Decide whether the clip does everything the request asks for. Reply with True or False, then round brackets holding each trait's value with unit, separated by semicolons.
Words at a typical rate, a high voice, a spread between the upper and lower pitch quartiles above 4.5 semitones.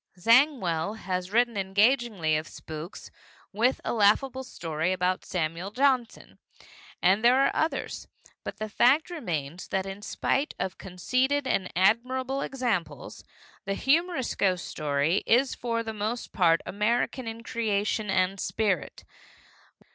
False (130 wpm; 210 Hz; 5.4 semitones)